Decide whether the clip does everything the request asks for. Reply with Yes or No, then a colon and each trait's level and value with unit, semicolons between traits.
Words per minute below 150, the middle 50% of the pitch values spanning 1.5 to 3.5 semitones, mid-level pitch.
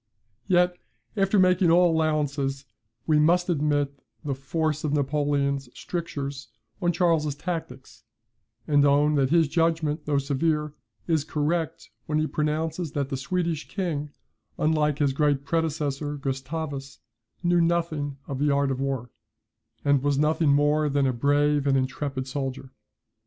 Yes: average, 140 wpm; narrow, 2.5 semitones; medium, 150 Hz